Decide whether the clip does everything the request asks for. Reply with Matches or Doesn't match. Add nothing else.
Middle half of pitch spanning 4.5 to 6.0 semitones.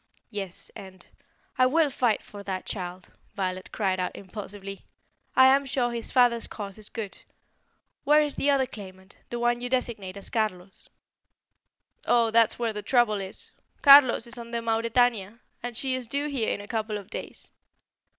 Doesn't match